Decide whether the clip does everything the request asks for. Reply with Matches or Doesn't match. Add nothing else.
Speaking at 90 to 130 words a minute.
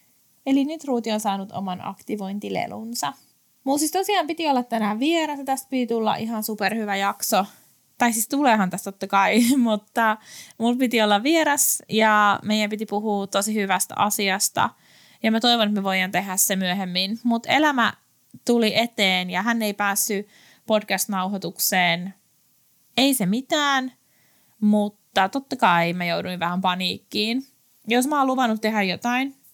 Doesn't match